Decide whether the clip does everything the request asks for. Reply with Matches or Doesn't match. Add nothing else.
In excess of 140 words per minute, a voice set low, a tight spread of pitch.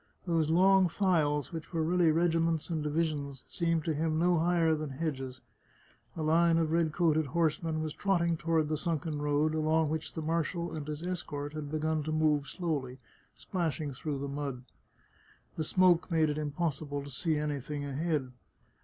Doesn't match